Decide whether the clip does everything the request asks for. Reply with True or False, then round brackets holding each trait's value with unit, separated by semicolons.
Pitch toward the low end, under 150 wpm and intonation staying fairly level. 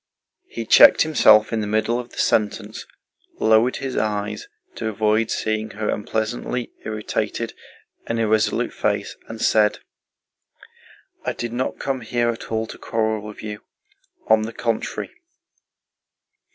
True (110 Hz; 135 wpm; 1.3 semitones)